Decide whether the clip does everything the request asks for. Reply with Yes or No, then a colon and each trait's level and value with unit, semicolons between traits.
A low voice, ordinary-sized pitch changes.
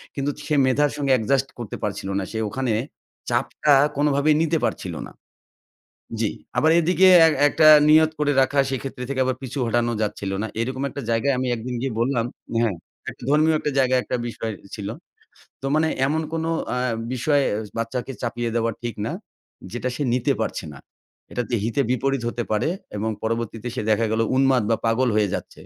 Yes: low, 130 Hz; average, 3.6 semitones